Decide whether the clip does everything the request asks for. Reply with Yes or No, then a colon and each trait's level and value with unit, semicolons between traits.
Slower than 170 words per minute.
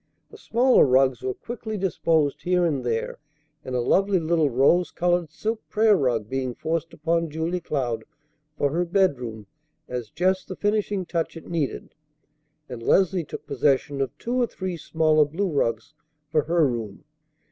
Yes: average, 160 wpm